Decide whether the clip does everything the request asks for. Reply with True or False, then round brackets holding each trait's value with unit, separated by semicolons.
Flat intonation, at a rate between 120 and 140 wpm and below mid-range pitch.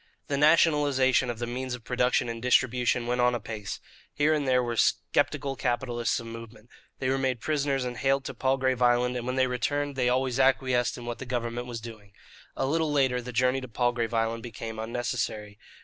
False (2.0 semitones; 195 wpm; 125 Hz)